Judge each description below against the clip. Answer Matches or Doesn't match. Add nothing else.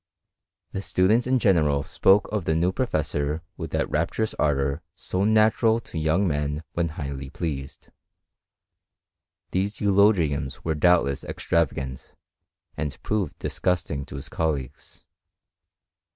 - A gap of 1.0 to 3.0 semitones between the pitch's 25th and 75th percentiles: Doesn't match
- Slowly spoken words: Matches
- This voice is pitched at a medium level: Doesn't match